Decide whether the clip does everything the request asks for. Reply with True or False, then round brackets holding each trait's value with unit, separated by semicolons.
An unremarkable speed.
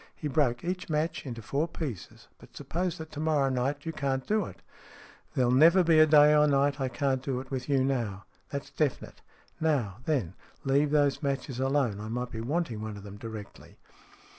False (210 wpm)